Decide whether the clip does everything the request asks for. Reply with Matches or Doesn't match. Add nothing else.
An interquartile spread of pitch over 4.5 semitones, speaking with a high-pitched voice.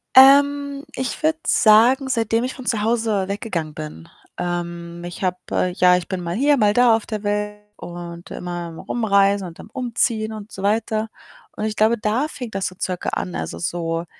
Matches